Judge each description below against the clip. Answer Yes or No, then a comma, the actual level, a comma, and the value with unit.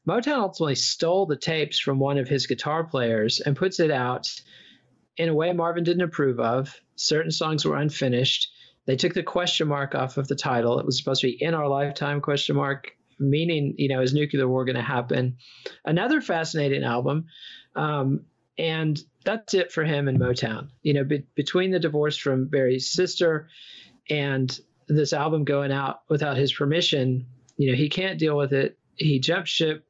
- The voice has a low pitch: No, medium, 145 Hz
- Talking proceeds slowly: No, average, 185 wpm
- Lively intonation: No, average, 3.2 semitones